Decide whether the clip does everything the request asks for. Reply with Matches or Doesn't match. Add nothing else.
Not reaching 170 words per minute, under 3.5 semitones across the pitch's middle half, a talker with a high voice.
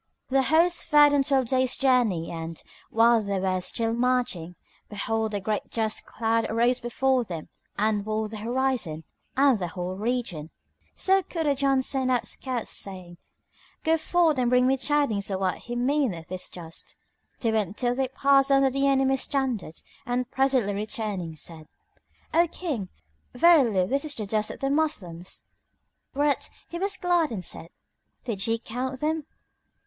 Doesn't match